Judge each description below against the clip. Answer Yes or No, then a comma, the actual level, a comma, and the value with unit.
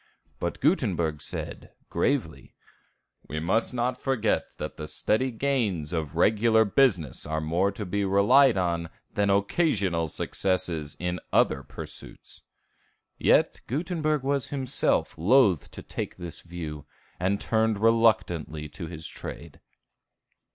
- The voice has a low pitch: Yes, low, 100 Hz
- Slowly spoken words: Yes, slow, 125 wpm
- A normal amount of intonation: No, wide, 6.3 semitones